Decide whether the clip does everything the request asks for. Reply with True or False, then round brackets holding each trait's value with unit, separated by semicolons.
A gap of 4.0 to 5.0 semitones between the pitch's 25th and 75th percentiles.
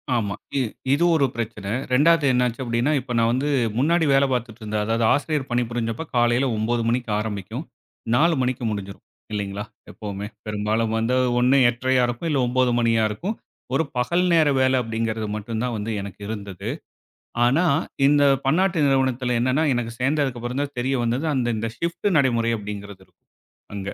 False (3.5 semitones)